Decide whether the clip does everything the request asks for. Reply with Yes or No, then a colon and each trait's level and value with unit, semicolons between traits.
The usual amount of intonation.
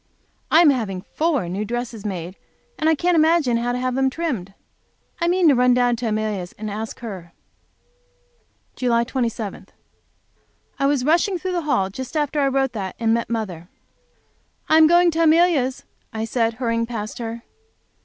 No: wide, 5.8 semitones